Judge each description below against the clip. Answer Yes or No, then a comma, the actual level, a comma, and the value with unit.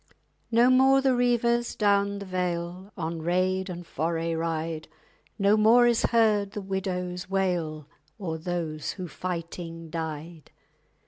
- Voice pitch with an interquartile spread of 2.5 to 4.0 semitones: Yes, average, 3.7 semitones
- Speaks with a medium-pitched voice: Yes, medium, 180 Hz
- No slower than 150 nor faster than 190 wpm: No, slow, 135 wpm